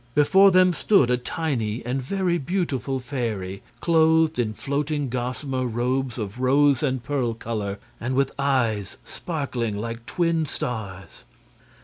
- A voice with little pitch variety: No, average, 4.2 semitones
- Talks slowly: Yes, slow, 130 wpm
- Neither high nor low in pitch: No, low, 130 Hz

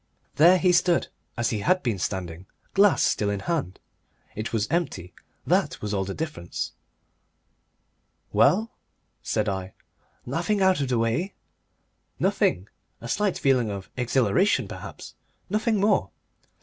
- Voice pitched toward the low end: Yes, low, 125 Hz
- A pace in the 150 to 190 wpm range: No, slow, 135 wpm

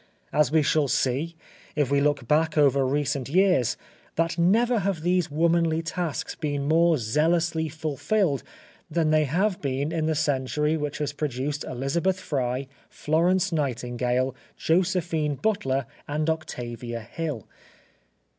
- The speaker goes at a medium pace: No, slow, 130 wpm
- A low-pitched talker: No, medium, 150 Hz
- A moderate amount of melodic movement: Yes, average, 3.4 semitones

